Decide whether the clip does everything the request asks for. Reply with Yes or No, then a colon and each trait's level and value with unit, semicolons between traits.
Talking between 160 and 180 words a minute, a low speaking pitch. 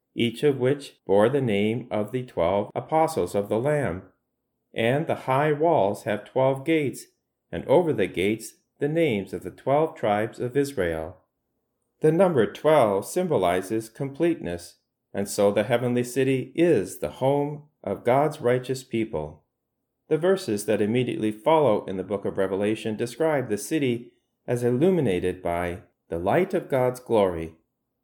No: average, 150 wpm; low, 125 Hz